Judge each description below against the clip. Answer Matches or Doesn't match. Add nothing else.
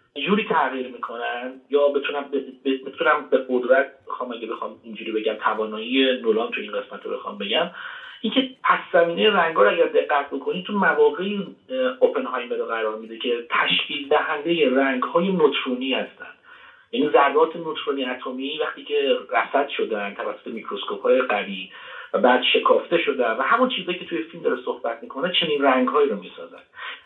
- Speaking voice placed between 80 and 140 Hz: Doesn't match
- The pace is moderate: Doesn't match